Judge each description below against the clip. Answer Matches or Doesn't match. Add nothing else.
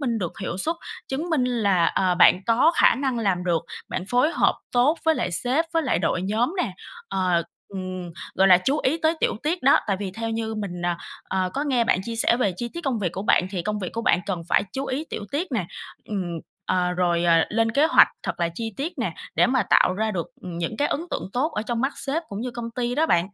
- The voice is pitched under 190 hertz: Doesn't match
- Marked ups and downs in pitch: Matches